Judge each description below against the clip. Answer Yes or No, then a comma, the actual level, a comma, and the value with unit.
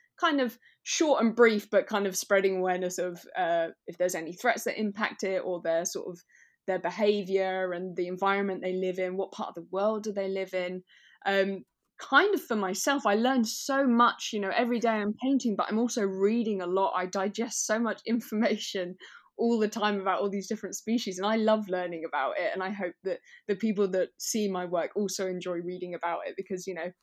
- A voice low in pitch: No, high, 200 Hz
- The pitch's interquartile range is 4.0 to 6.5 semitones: No, average, 3.3 semitones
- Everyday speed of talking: No, fast, 220 wpm